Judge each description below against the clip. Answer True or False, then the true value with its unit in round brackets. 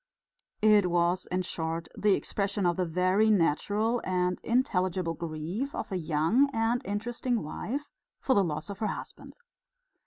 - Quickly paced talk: False (150 wpm)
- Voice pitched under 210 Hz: True (190 Hz)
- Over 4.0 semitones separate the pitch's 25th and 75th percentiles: True (4.4 semitones)